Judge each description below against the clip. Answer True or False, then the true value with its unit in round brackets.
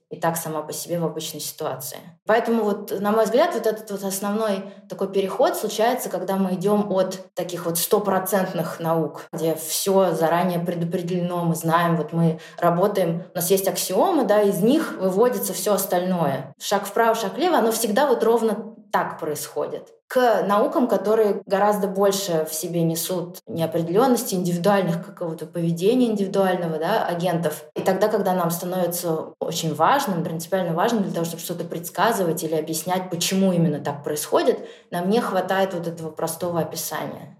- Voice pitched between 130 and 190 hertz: True (185 Hz)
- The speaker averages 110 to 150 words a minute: False (160 wpm)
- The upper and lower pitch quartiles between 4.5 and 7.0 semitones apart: False (3.5 semitones)